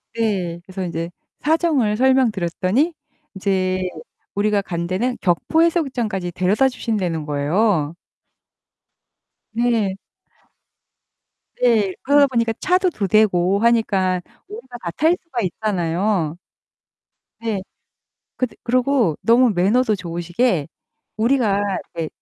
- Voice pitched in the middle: No, high, 210 Hz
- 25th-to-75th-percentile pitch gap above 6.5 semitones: No, wide, 5.4 semitones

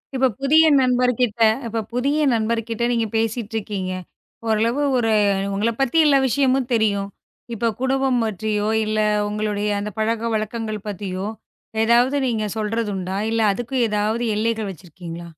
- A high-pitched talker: Yes, high, 225 Hz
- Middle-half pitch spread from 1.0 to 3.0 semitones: Yes, narrow, 2.6 semitones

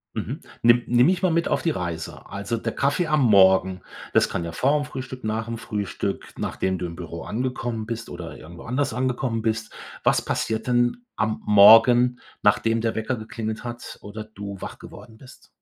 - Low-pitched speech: Yes, low, 115 Hz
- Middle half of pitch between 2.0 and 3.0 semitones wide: No, average, 3.5 semitones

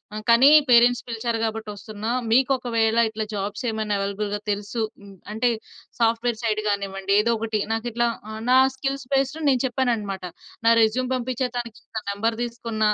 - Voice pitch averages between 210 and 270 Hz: Yes, high, 225 Hz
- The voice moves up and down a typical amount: No, narrow, 2.2 semitones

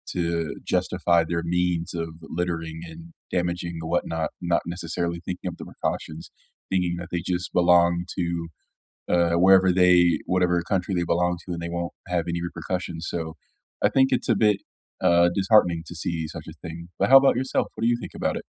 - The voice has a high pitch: No, very low, 85 Hz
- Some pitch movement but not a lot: No, narrow, 1.2 semitones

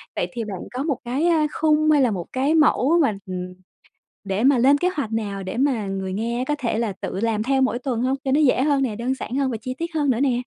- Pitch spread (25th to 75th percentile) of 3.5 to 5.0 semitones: Yes, average, 4.3 semitones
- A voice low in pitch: No, very high, 255 Hz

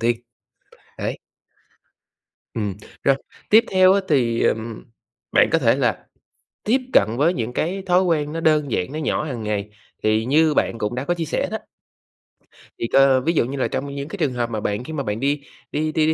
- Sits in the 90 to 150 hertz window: Yes, medium, 140 Hz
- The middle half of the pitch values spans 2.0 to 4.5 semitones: No, wide, 5.4 semitones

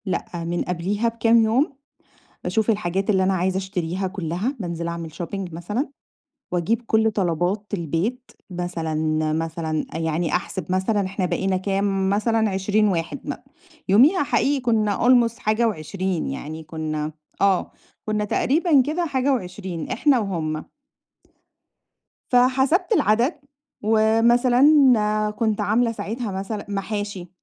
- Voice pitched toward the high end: Yes, high, 200 Hz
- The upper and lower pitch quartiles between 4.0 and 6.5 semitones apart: Yes, average, 4.6 semitones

